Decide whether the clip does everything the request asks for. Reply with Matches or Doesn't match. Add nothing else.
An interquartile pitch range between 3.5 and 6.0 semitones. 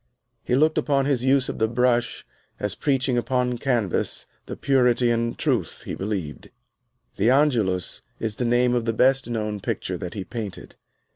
Doesn't match